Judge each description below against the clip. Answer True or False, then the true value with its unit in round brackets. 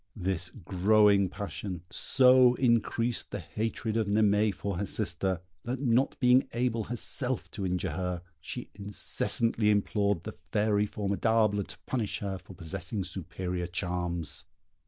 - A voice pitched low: True (105 Hz)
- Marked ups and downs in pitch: False (3.7 semitones)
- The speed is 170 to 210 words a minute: False (135 wpm)